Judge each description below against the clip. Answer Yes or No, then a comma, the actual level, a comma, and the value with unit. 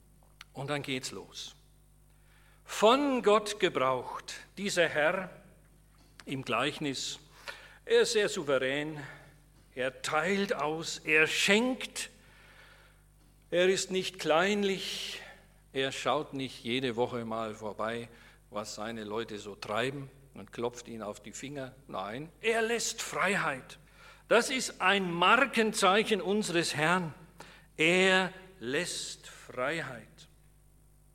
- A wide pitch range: Yes, wide, 6.5 semitones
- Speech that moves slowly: Yes, slow, 105 wpm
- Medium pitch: Yes, medium, 155 Hz